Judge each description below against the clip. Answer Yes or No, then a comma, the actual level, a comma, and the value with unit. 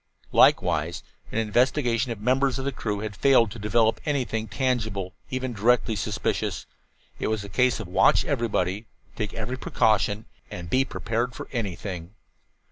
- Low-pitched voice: Yes, low, 115 Hz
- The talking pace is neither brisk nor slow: Yes, average, 155 wpm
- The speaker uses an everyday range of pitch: Yes, average, 3.5 semitones